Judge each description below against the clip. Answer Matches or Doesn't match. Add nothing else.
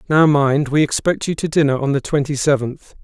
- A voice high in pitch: Doesn't match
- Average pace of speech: Doesn't match